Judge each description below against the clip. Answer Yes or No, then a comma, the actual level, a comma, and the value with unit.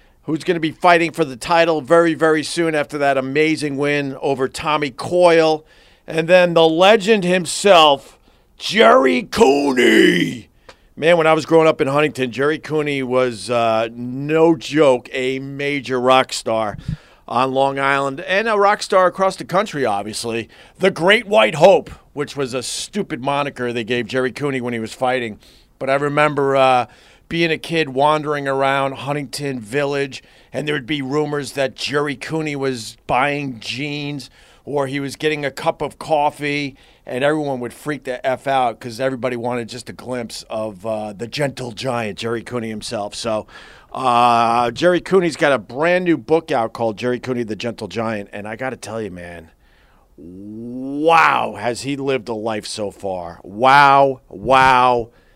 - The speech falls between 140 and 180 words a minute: Yes, average, 170 wpm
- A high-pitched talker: No, low, 135 Hz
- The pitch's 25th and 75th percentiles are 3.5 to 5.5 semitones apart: Yes, average, 4.2 semitones